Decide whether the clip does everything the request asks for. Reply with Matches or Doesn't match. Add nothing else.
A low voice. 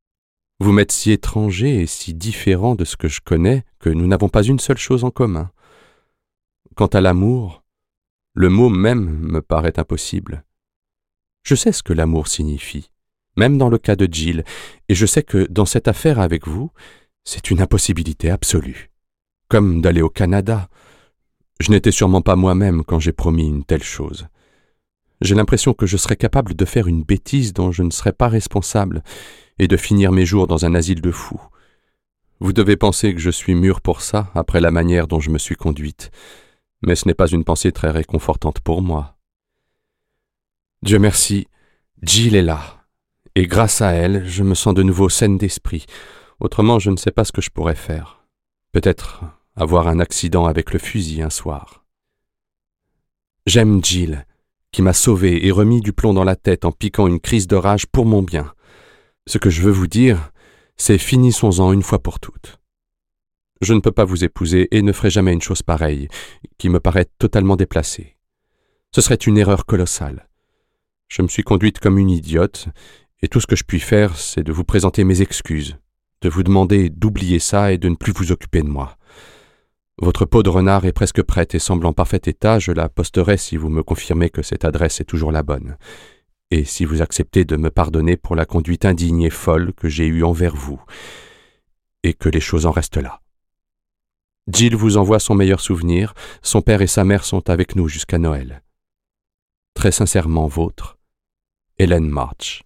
Matches